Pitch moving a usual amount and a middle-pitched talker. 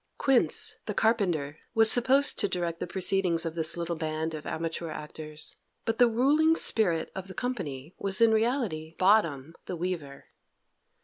No: wide, 5.9 semitones; medium, 180 Hz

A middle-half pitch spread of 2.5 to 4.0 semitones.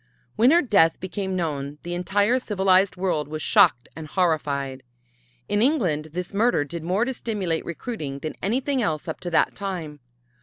No: average, 5.0 semitones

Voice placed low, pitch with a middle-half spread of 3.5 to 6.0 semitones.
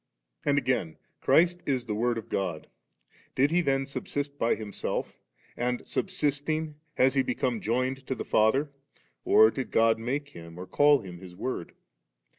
Yes: low, 130 Hz; average, 4.5 semitones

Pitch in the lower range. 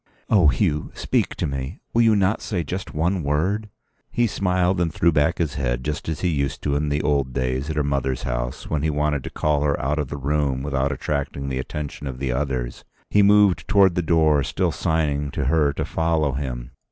Yes: very low, 75 Hz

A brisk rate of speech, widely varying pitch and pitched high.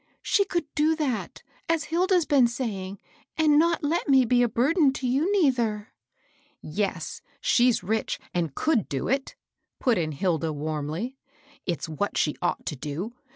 No: average, 170 wpm; wide, 9.0 semitones; high, 245 Hz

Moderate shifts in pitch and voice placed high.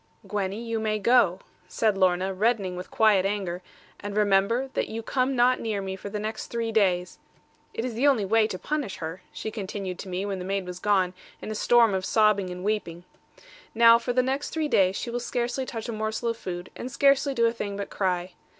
Yes: average, 3.6 semitones; high, 210 Hz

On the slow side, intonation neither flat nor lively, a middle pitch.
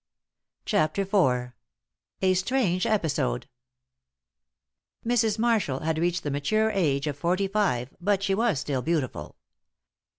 No: slow, 120 wpm; wide, 6.3 semitones; medium, 180 Hz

